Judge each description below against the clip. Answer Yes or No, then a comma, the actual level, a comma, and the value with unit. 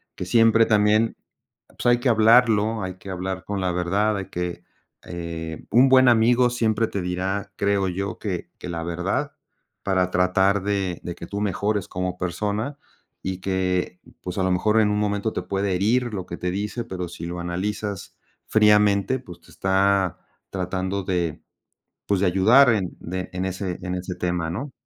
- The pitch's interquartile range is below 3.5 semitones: Yes, average, 2.8 semitones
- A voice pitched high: No, very low, 95 Hz